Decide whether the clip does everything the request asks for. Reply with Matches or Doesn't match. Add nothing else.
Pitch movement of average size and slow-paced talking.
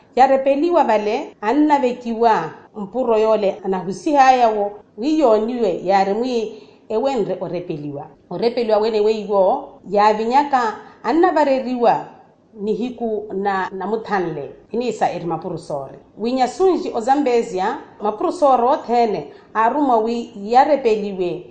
Matches